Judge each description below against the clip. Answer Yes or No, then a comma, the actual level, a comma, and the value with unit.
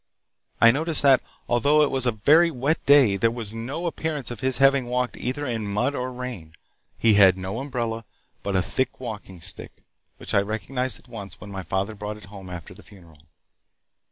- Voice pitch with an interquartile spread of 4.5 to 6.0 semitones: Yes, average, 4.8 semitones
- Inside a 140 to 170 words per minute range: No, average, 195 wpm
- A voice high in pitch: No, low, 115 Hz